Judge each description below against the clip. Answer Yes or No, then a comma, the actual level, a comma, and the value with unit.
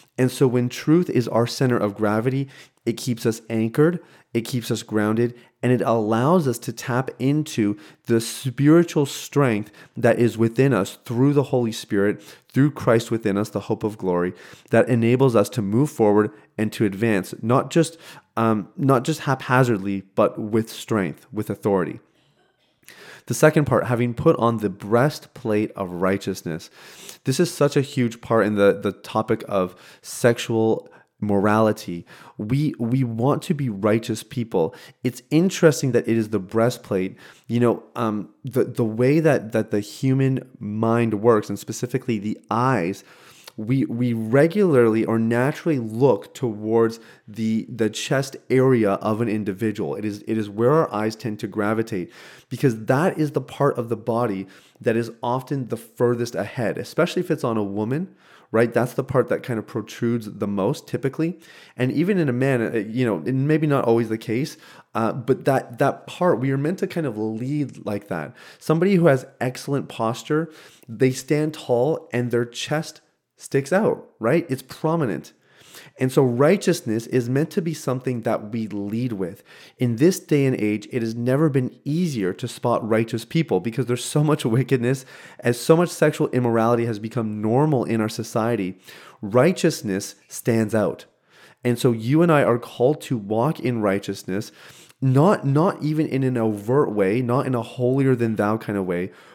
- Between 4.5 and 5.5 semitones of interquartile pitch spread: No, average, 3.9 semitones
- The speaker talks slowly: No, average, 175 wpm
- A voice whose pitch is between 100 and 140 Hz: Yes, low, 120 Hz